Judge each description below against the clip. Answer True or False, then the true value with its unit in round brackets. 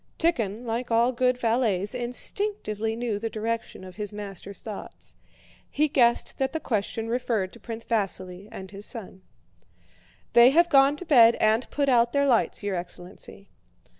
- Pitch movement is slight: False (3.6 semitones)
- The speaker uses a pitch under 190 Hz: False (230 Hz)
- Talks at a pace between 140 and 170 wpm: True (160 wpm)